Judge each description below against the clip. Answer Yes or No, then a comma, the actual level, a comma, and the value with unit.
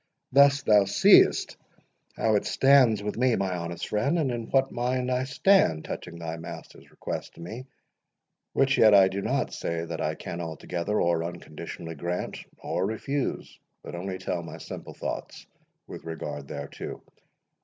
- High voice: No, low, 100 Hz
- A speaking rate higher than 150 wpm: Yes, average, 160 wpm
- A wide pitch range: Yes, wide, 6.9 semitones